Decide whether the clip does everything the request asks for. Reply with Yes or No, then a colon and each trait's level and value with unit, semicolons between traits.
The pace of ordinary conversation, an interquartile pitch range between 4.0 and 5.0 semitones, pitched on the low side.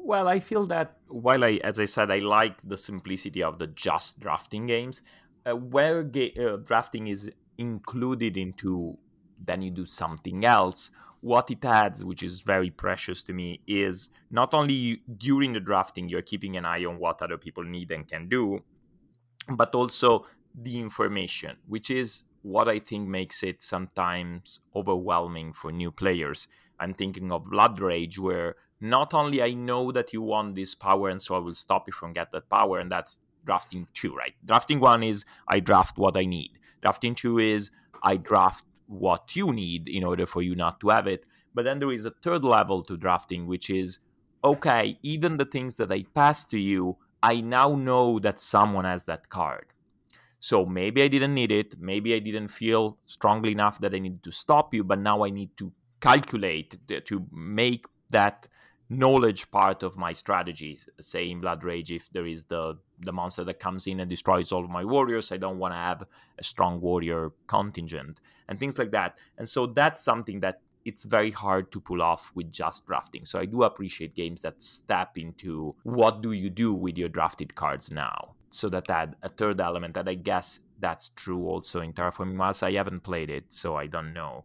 Yes: average, 195 wpm; average, 4.3 semitones; very low, 95 Hz